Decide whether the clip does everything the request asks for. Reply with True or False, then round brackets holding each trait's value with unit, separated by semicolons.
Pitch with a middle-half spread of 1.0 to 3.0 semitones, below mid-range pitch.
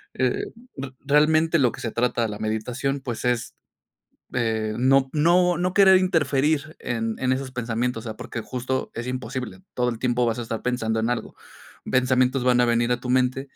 True (2.7 semitones; 125 Hz)